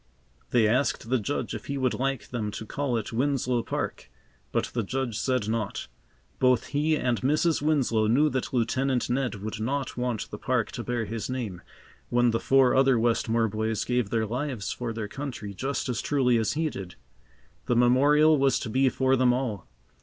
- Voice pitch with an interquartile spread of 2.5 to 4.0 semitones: Yes, average, 3.1 semitones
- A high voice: No, low, 125 Hz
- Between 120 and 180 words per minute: No, average, 190 wpm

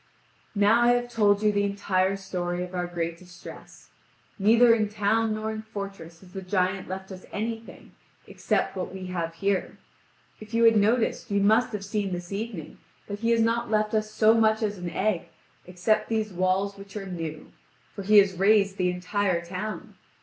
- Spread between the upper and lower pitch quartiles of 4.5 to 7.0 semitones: No, average, 2.8 semitones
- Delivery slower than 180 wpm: No, average, 185 wpm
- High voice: Yes, high, 200 Hz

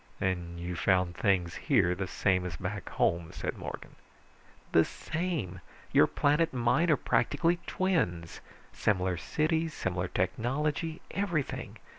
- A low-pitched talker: Yes, very low, 95 Hz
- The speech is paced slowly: Yes, slow, 130 wpm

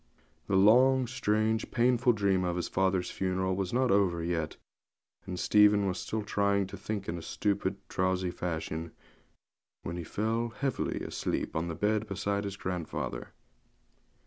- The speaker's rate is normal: Yes, average, 145 wpm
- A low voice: Yes, low, 100 Hz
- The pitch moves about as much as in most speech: Yes, average, 3.0 semitones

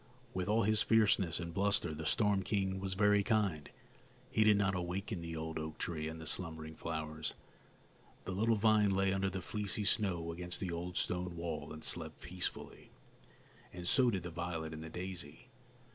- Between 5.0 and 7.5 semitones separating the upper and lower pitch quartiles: No, average, 3.6 semitones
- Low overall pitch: Yes, very low, 90 Hz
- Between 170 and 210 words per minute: Yes, average, 180 wpm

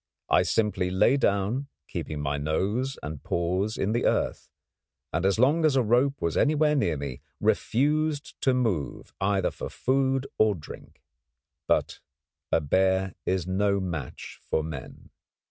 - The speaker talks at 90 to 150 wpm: Yes, average, 145 wpm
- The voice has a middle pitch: No, low, 100 Hz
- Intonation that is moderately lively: No, wide, 7.6 semitones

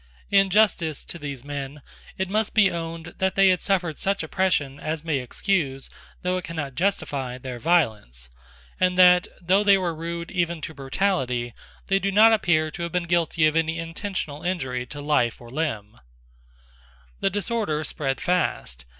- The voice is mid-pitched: Yes, medium, 165 Hz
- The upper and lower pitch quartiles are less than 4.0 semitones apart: No, average, 4.8 semitones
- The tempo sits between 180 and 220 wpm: No, average, 165 wpm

